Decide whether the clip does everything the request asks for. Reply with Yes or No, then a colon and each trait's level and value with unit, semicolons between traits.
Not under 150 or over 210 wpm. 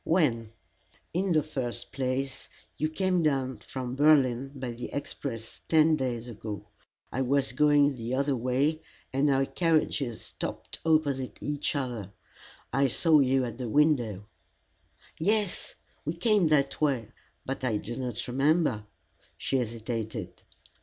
No: average, 140 wpm